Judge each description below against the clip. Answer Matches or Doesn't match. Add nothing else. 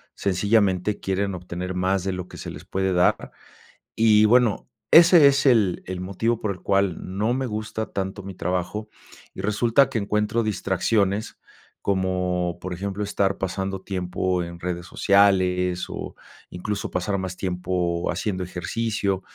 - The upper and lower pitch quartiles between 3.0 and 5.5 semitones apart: Doesn't match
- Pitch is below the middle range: Matches